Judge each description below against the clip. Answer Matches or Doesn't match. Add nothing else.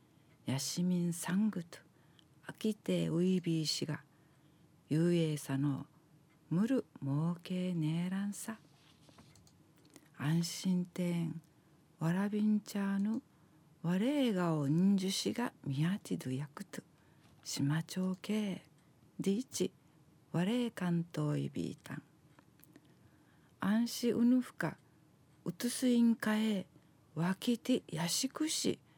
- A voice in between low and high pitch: Matches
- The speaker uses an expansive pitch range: Doesn't match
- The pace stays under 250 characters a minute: Matches